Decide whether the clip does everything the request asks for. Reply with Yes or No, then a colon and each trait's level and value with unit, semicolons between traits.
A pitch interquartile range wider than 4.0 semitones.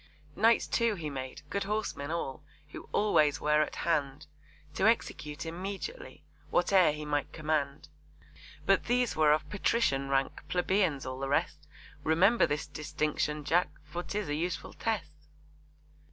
Yes: average, 4.7 semitones